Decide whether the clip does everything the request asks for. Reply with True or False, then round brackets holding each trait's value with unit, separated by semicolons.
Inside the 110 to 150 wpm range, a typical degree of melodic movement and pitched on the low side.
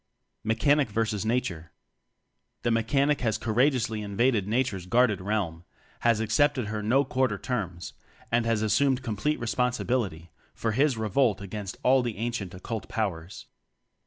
True (140 wpm; 3.5 semitones; 110 Hz)